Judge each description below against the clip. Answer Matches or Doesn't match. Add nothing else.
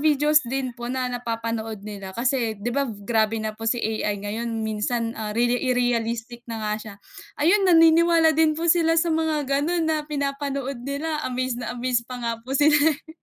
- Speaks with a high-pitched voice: Matches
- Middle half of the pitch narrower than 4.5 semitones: Doesn't match